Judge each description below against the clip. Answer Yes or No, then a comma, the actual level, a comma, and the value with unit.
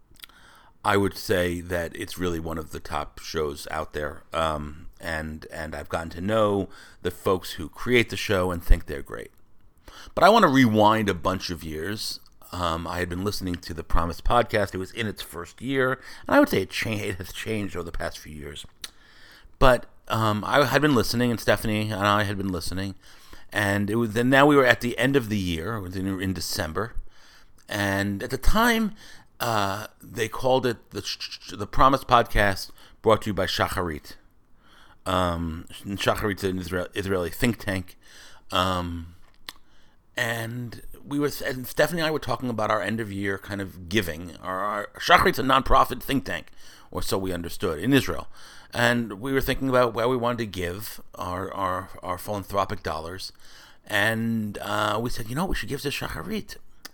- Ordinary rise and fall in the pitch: Yes, average, 4.9 semitones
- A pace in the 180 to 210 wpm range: Yes, average, 185 wpm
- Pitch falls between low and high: No, low, 100 Hz